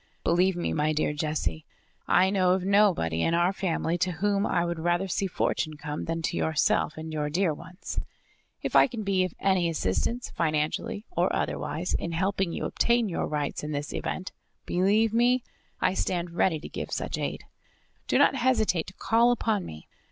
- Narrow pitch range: No, average, 4.0 semitones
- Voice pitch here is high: No, medium, 175 Hz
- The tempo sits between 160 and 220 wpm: Yes, average, 185 wpm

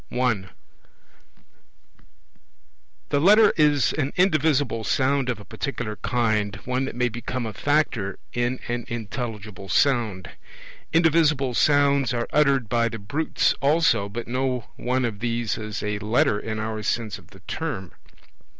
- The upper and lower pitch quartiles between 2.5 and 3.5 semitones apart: No, average, 4.5 semitones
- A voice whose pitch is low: Yes, low, 120 Hz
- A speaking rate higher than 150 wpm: No, average, 140 wpm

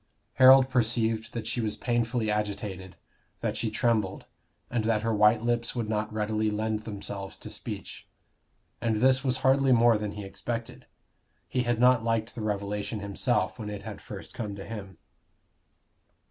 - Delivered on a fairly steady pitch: Yes, narrow, 2.3 semitones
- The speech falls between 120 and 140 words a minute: No, average, 160 wpm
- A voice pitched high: No, low, 110 Hz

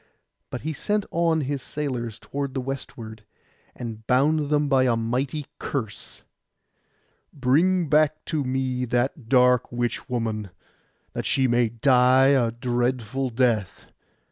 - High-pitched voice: No, low, 130 Hz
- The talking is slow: Yes, slow, 125 wpm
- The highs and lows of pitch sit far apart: No, average, 2.9 semitones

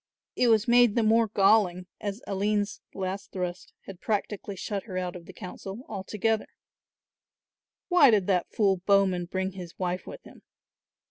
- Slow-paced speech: No, average, 155 wpm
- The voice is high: Yes, high, 195 Hz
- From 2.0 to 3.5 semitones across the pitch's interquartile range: Yes, average, 2.7 semitones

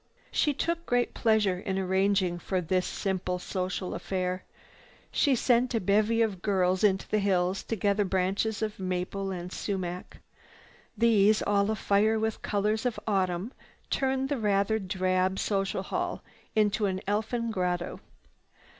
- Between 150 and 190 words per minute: No, average, 140 wpm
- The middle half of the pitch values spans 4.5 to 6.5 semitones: No, average, 2.9 semitones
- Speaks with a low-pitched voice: No, high, 200 Hz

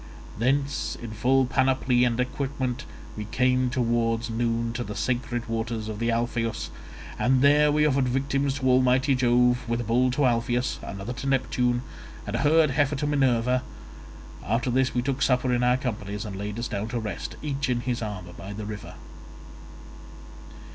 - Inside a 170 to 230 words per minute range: Yes, average, 175 wpm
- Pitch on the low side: Yes, low, 125 Hz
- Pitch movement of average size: No, narrow, 2.3 semitones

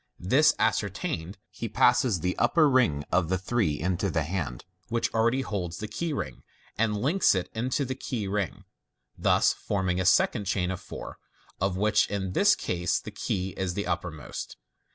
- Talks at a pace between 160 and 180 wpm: Yes, average, 175 wpm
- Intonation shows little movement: No, average, 4.6 semitones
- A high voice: No, very low, 95 Hz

